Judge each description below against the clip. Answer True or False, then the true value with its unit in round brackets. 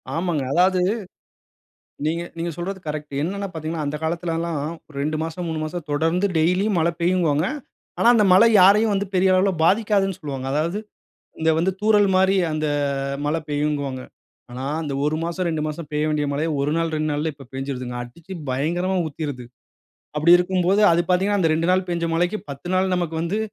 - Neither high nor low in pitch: True (165 Hz)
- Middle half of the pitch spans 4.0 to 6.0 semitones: False (3.5 semitones)